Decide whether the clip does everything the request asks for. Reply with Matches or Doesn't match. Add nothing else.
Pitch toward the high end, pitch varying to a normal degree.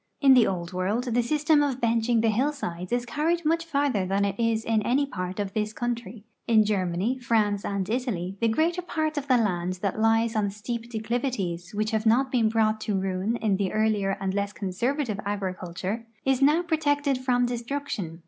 Matches